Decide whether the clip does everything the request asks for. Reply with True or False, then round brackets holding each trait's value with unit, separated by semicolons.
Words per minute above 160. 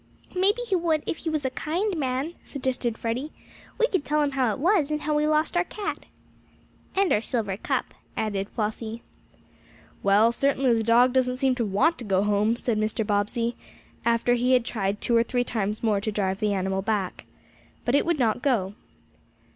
True (195 wpm)